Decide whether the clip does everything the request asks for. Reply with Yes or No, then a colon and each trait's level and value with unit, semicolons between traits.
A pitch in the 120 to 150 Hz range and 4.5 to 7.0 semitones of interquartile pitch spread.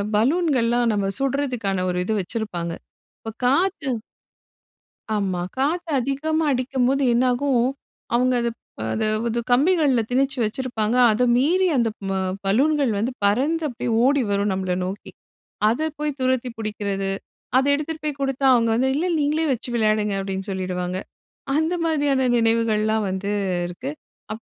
No: high, 245 Hz; average, 4.8 semitones